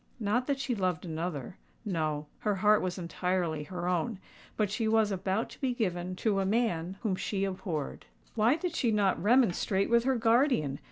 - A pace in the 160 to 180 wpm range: Yes, average, 170 wpm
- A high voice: Yes, high, 195 Hz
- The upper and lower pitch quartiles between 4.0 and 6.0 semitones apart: Yes, average, 4.3 semitones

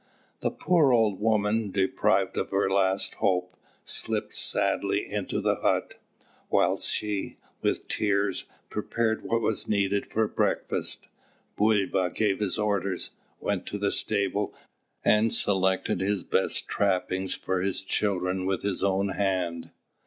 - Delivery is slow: Yes, slow, 130 wpm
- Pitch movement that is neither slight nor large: No, narrow, 1.8 semitones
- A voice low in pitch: Yes, low, 100 Hz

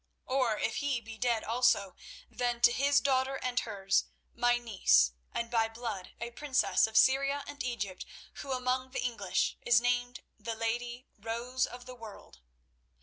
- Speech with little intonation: Yes, narrow, 2.2 semitones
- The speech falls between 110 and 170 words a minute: Yes, average, 160 wpm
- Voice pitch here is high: Yes, high, 240 Hz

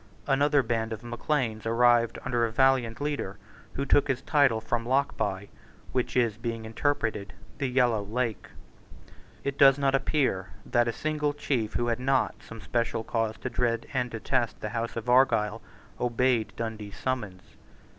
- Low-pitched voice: Yes, low, 120 Hz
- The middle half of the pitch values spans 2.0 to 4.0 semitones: Yes, average, 2.9 semitones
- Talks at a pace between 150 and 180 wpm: Yes, average, 155 wpm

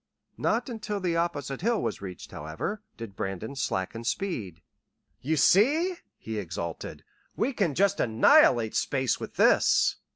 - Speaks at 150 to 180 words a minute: No, slow, 135 wpm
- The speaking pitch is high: No, medium, 140 Hz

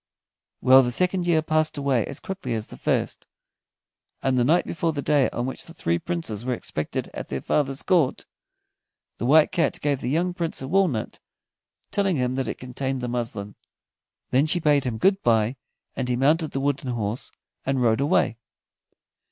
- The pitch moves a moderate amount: Yes, average, 4.4 semitones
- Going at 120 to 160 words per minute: No, average, 185 wpm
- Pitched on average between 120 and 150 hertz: Yes, low, 135 Hz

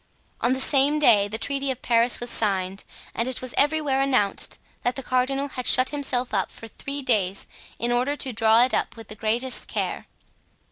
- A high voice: Yes, very high, 250 Hz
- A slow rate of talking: No, average, 195 wpm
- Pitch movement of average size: Yes, average, 3.3 semitones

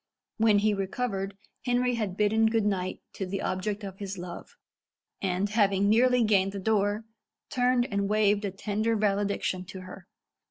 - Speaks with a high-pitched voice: Yes, high, 205 Hz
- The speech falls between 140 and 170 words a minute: Yes, average, 160 wpm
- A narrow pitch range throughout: Yes, narrow, 2.2 semitones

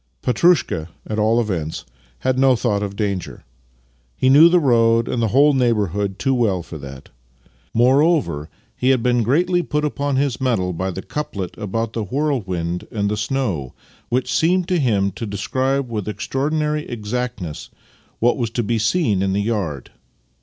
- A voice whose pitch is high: No, low, 115 Hz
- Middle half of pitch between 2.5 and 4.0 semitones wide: No, average, 5.1 semitones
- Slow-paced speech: No, average, 165 wpm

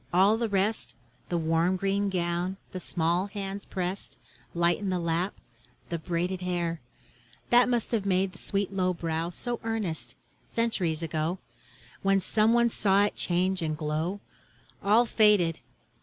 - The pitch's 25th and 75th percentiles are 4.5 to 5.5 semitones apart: No, average, 3.0 semitones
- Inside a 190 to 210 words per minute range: No, average, 150 wpm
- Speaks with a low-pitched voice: No, medium, 185 Hz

